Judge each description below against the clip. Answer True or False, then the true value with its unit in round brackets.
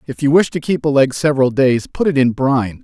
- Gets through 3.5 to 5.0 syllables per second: False (5.9 syllables/s)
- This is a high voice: False (135 Hz)